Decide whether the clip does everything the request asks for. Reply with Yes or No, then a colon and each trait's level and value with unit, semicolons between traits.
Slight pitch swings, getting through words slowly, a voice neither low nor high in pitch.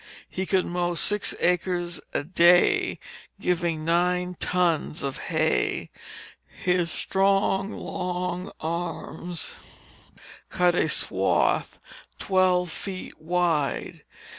Yes: narrow, 1.1 semitones; slow, 90 wpm; medium, 180 Hz